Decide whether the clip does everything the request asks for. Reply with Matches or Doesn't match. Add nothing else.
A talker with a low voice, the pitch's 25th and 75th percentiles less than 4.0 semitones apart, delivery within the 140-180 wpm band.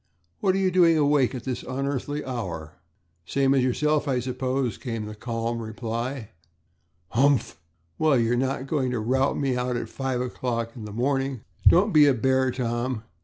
Matches